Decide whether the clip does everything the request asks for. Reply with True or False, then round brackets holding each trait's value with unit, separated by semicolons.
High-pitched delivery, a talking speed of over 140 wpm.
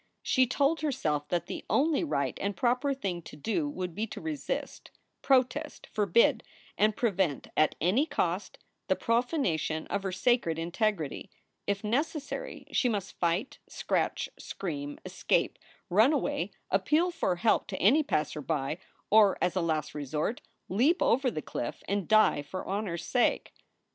True (205 Hz; 155 wpm)